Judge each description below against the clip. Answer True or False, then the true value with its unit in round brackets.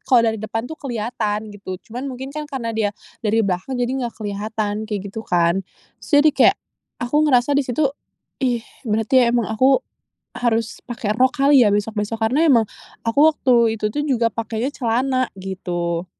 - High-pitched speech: True (230 Hz)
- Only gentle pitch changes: False (3.4 semitones)